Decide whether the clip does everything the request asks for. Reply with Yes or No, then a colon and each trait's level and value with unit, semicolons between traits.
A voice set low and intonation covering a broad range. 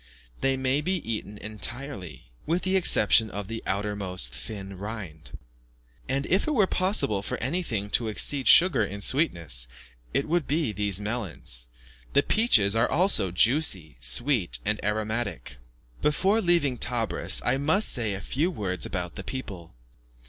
Yes: low, 110 Hz; wide, 6.8 semitones